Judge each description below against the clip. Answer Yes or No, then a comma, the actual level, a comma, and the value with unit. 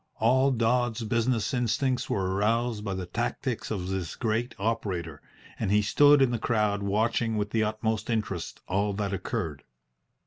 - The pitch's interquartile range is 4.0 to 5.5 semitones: No, average, 3.0 semitones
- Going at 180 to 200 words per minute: No, average, 160 wpm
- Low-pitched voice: Yes, low, 110 Hz